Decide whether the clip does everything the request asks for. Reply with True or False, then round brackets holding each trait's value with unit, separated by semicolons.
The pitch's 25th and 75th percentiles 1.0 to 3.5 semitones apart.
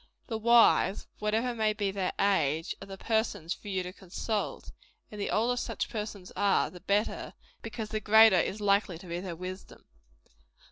True (2.8 semitones)